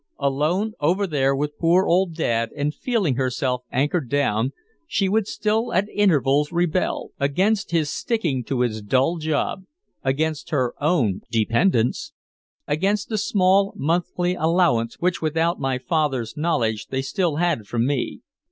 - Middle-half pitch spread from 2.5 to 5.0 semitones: No, wide, 5.4 semitones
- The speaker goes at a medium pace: Yes, average, 145 wpm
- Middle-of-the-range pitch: Yes, medium, 155 Hz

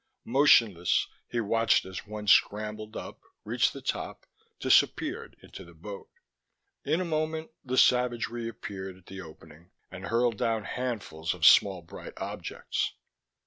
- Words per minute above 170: No, average, 140 wpm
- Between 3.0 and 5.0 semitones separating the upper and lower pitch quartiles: Yes, average, 4.3 semitones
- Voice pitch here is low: Yes, low, 105 Hz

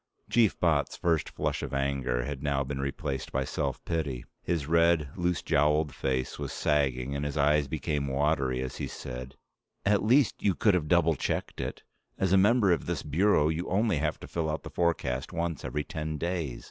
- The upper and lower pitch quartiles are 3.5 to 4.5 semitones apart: Yes, average, 3.9 semitones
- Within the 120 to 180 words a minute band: No, average, 195 wpm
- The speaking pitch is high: No, very low, 75 Hz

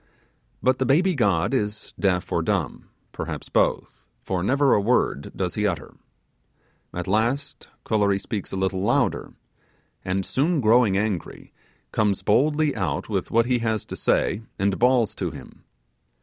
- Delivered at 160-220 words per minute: No, average, 150 wpm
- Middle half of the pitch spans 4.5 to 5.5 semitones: Yes, average, 4.9 semitones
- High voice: No, low, 105 Hz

